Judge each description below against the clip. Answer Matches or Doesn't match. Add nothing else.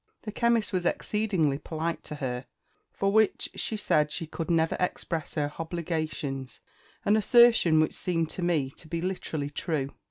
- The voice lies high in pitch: Doesn't match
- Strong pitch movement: Doesn't match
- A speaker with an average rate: Matches